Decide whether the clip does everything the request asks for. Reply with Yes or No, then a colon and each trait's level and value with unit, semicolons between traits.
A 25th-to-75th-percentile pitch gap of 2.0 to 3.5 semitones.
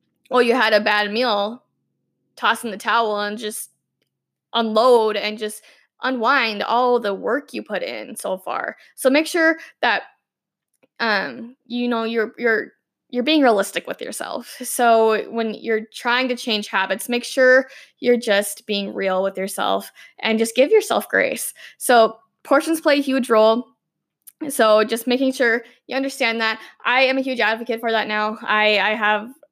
Yes: average, 3.1 semitones